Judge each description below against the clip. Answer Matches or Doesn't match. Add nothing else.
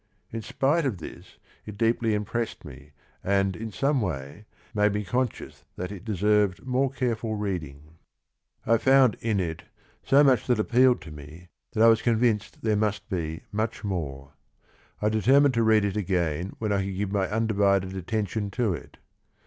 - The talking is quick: Doesn't match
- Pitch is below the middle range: Matches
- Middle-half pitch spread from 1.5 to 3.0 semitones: Doesn't match